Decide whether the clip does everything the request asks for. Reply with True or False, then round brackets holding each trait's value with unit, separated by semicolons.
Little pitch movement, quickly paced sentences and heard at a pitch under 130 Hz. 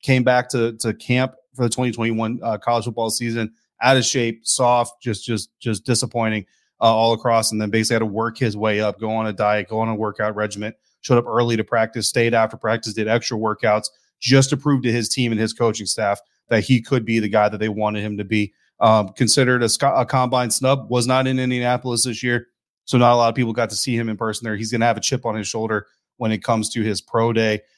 True (2.0 semitones; 250 wpm; 115 Hz)